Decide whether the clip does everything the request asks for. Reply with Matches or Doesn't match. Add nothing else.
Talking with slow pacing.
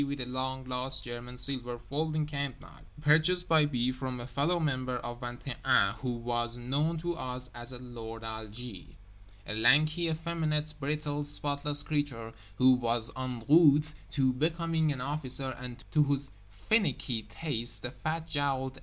Doesn't match